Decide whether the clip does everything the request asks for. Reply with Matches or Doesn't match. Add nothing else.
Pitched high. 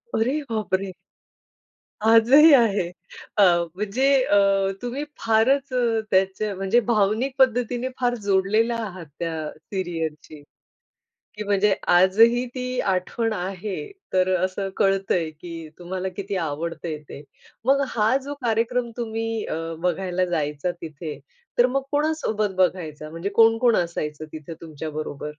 Matches